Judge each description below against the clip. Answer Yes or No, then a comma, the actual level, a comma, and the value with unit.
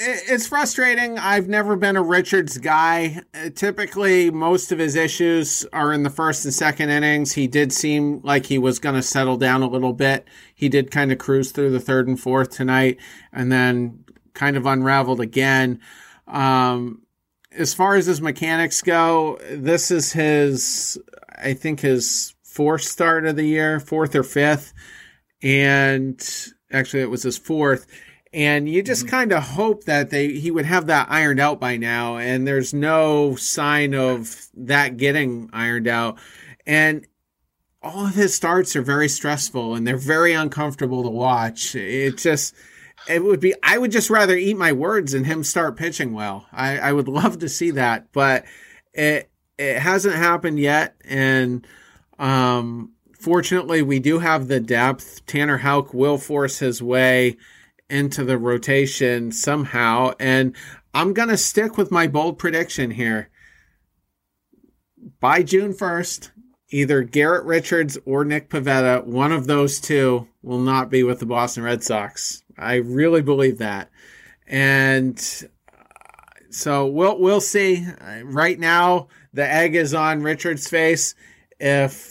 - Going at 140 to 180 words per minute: Yes, average, 155 wpm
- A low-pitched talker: No, medium, 145 Hz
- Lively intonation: No, average, 4.2 semitones